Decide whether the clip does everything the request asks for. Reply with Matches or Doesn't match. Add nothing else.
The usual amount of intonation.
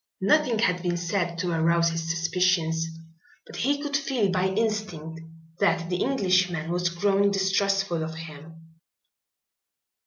Matches